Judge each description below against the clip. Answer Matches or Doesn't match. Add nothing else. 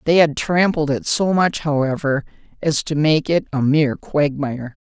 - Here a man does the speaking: Doesn't match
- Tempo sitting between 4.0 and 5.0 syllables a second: Matches